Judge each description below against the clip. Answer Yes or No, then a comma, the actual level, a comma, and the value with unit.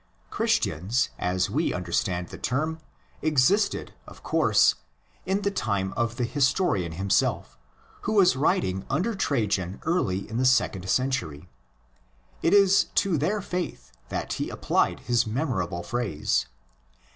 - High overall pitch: No, low, 125 Hz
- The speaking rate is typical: No, slow, 130 wpm